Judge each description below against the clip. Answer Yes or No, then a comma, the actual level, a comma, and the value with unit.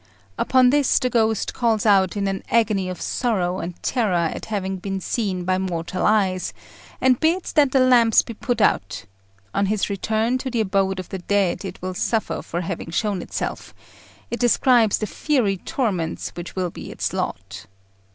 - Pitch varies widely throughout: No, average, 4.3 semitones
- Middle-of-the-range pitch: No, high, 200 Hz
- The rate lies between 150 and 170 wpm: No, average, 180 wpm